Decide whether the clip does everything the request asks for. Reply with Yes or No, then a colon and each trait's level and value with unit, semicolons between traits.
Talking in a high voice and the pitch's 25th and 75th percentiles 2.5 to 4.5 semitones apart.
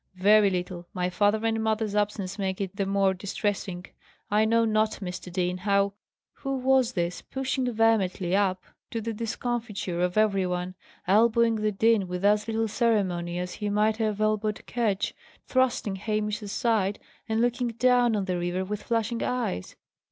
Yes: high, 210 Hz; average, 3.1 semitones